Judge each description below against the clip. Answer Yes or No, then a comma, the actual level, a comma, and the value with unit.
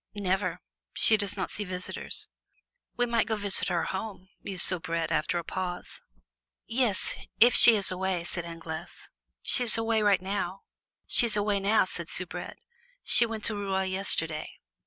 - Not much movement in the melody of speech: No, average, 3.3 semitones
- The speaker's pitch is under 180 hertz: No, high, 195 Hz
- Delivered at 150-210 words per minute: No, slow, 135 wpm